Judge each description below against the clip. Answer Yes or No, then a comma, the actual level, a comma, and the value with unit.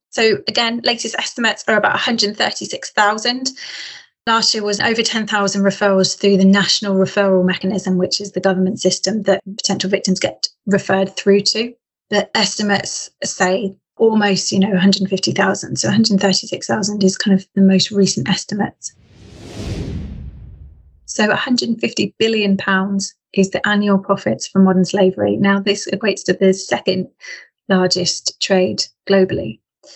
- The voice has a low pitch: No, high, 195 Hz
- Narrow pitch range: Yes, narrow, 1.5 semitones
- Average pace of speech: No, slow, 130 wpm